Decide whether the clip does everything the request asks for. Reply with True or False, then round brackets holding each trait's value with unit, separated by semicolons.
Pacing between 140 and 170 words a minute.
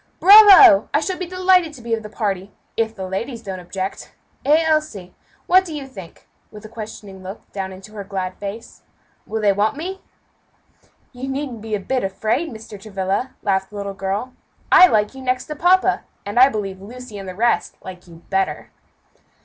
False (190 wpm)